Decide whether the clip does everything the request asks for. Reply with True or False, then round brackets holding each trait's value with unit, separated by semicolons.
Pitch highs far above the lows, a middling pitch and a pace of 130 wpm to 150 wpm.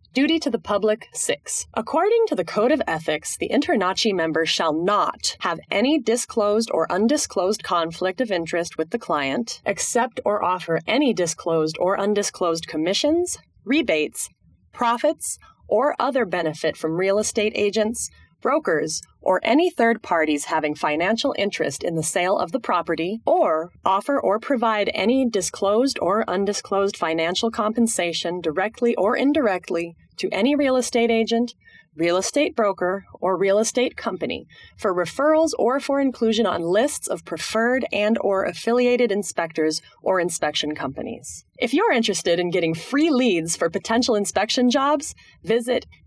False (5.9 semitones; 215 Hz; 145 wpm)